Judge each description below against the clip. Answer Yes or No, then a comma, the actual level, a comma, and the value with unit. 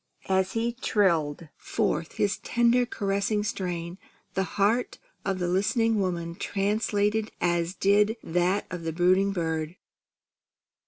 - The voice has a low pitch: No, high, 195 Hz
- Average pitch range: Yes, average, 3.1 semitones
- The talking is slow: Yes, slow, 120 wpm